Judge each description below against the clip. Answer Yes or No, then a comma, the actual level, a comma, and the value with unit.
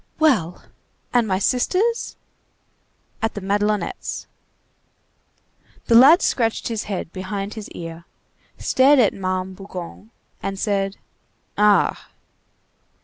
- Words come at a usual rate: No, slow, 100 wpm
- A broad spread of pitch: No, average, 3.7 semitones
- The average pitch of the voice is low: No, high, 205 Hz